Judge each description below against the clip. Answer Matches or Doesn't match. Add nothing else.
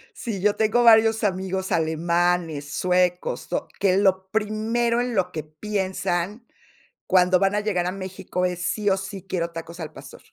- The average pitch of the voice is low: Doesn't match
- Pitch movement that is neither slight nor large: Matches